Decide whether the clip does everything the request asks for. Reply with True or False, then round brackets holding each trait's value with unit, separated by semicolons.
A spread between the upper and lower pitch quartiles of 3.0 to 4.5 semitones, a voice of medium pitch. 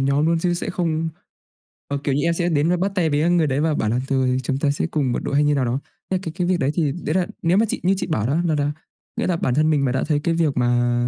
True (3.8 semitones; 150 Hz)